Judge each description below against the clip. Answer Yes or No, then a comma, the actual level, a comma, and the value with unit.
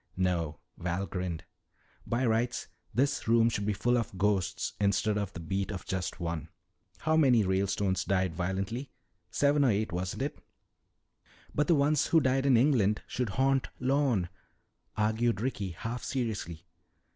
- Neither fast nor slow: Yes, average, 150 wpm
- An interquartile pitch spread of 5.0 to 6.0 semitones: Yes, wide, 5.4 semitones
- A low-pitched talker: Yes, low, 105 Hz